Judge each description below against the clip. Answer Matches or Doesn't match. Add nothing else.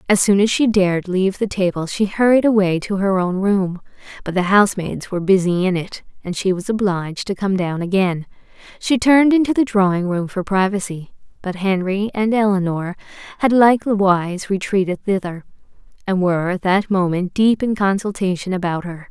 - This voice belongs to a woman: Matches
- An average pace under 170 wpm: Doesn't match